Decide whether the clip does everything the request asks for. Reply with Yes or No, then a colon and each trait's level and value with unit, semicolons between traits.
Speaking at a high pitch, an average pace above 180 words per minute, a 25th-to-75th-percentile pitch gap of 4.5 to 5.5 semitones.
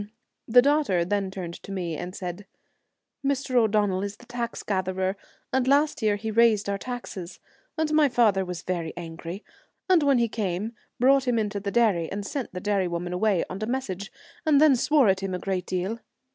Yes: high, 205 Hz; average, 200 wpm; average, 4.9 semitones